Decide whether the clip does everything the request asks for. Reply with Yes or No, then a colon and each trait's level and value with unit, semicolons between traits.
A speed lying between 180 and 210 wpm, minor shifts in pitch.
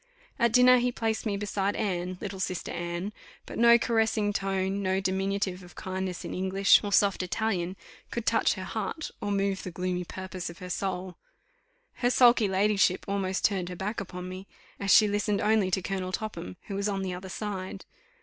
Yes: average, 190 wpm; narrow, 2.0 semitones